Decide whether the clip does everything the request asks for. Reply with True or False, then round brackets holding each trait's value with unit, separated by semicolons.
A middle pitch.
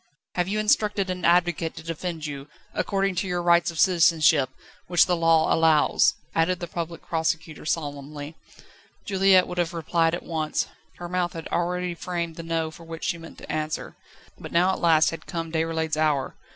True (165 Hz)